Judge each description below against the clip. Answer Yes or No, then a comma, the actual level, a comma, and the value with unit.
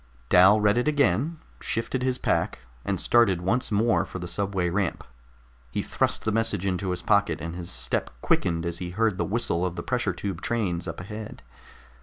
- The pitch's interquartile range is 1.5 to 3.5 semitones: No, average, 4.3 semitones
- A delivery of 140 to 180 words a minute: No, average, 190 wpm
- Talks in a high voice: No, low, 100 Hz